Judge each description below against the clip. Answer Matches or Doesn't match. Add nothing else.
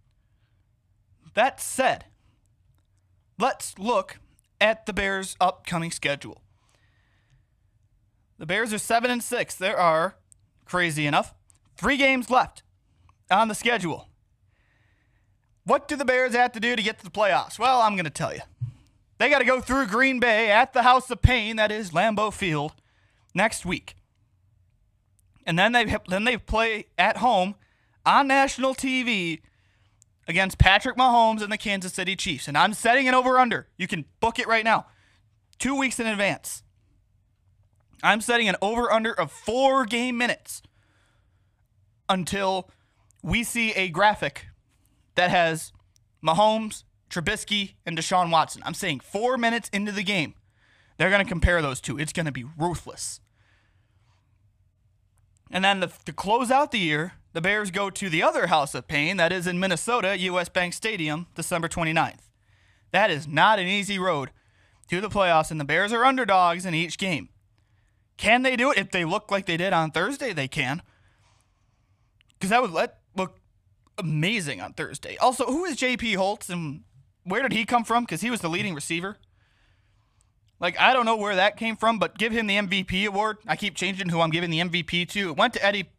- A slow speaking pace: Doesn't match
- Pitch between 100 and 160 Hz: Doesn't match